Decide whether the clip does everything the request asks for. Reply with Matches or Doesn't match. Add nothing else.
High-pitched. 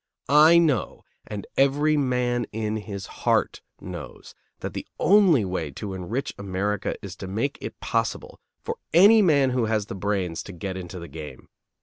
Doesn't match